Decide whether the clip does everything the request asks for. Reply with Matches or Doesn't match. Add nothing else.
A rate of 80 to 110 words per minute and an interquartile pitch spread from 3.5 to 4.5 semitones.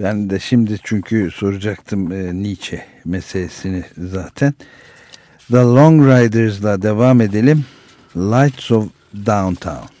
Matches